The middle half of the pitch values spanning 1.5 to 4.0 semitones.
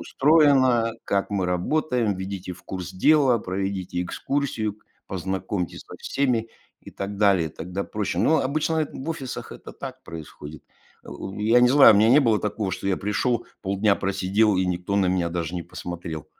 No: average, 5.0 semitones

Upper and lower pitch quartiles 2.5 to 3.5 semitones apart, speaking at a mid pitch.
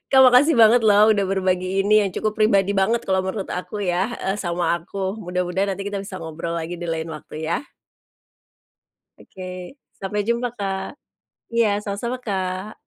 No: average, 2.8 semitones; high, 195 Hz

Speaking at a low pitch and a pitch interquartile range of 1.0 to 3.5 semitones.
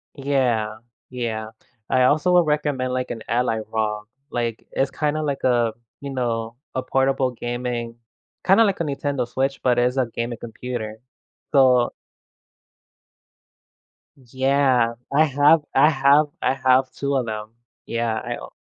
Yes: low, 130 Hz; average, 2.9 semitones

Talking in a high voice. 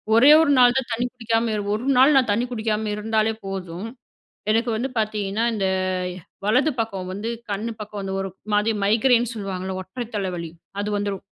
Yes: high, 215 Hz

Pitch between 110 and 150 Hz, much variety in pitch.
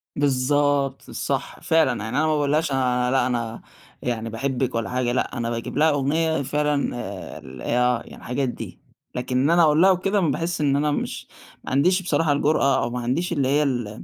No: low, 135 Hz; average, 3.4 semitones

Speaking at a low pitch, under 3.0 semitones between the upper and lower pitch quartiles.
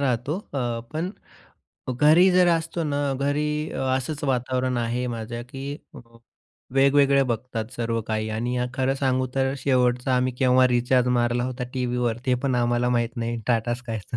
Yes: low, 125 Hz; narrow, 2.4 semitones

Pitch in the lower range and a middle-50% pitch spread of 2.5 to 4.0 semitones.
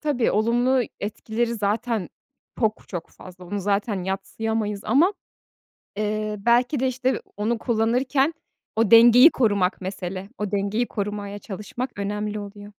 No: high, 215 Hz; average, 2.9 semitones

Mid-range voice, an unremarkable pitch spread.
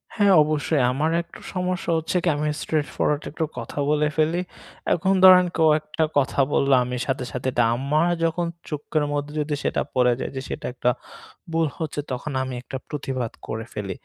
Yes: medium, 150 Hz; average, 3.5 semitones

